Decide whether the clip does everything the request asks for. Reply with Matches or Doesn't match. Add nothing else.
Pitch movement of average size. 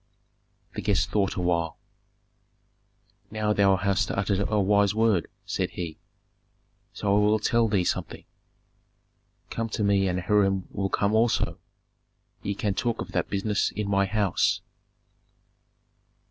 Doesn't match